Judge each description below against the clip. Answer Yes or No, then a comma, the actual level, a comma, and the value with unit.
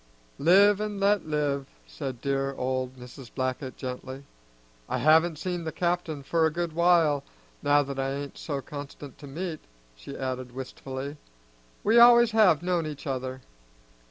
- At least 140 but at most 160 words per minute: Yes, average, 155 wpm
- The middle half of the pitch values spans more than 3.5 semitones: Yes, average, 4.5 semitones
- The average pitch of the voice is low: No, medium, 145 Hz